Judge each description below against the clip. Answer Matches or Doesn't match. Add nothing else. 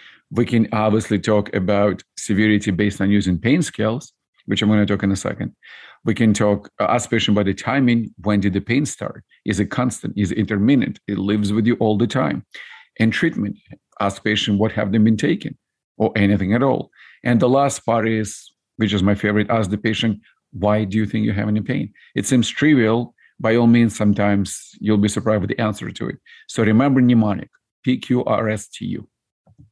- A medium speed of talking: Matches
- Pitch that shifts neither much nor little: Doesn't match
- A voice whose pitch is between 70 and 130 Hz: Matches